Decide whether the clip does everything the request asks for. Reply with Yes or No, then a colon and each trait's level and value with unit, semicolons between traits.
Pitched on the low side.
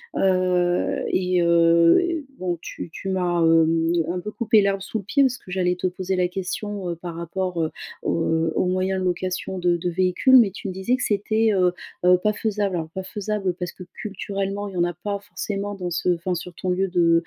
No: medium, 185 Hz